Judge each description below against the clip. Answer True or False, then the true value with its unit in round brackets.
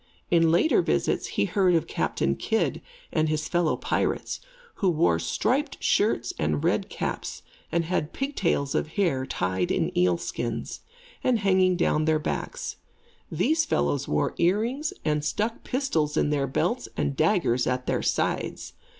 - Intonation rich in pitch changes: True (6.9 semitones)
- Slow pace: False (150 wpm)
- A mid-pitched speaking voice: True (160 Hz)